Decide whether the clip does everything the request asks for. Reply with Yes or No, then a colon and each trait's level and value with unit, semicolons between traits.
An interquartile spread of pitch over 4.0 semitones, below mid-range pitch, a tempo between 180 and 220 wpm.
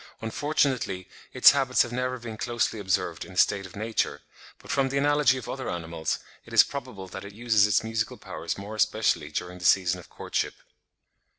Yes: average, 5.0 semitones; low, 110 Hz; average, 190 wpm